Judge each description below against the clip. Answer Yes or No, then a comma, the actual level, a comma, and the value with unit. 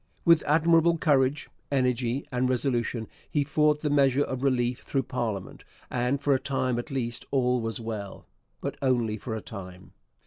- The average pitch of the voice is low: Yes, low, 130 Hz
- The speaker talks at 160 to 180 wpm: Yes, average, 165 wpm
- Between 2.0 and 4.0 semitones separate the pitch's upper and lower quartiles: Yes, average, 3.1 semitones